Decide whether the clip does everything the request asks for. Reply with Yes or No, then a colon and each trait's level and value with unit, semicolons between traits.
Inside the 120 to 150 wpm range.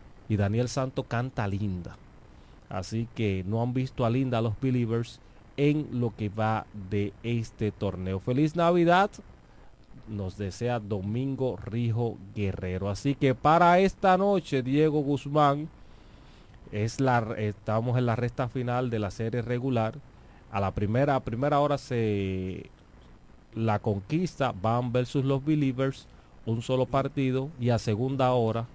Yes: average, 140 wpm